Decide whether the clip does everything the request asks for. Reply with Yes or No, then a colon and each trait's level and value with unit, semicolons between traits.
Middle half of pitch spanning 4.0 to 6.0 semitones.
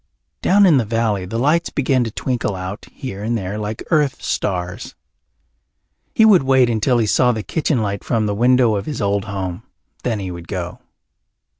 Yes: average, 4.5 semitones